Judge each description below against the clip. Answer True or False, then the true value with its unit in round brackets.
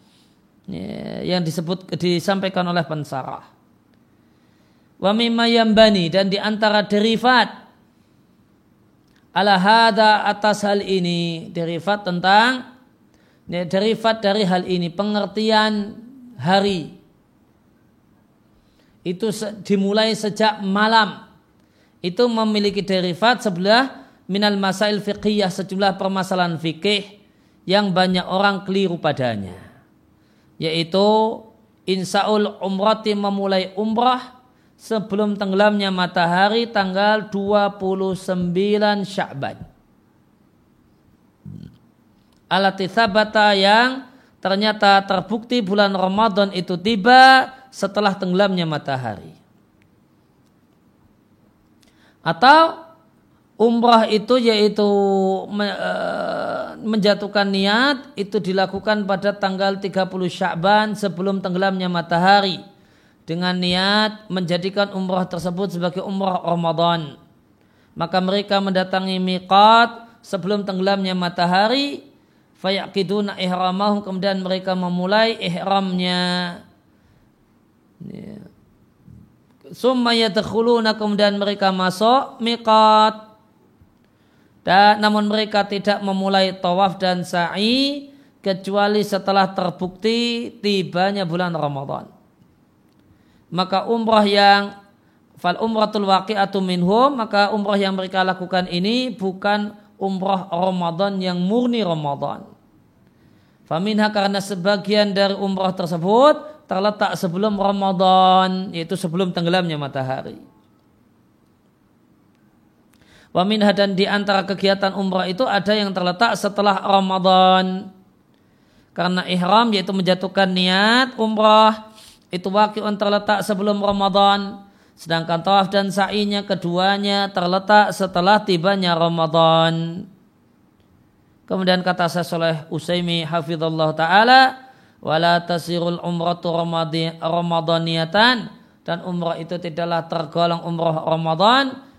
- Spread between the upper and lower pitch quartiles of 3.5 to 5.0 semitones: False (2.6 semitones)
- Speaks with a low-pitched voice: False (195 Hz)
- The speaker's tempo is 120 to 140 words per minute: False (85 wpm)